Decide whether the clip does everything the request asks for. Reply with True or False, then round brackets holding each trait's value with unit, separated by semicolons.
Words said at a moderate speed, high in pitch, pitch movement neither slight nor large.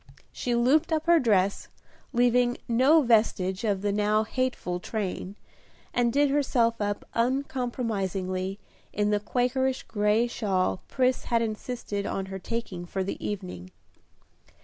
False (130 wpm; 230 Hz; 4.1 semitones)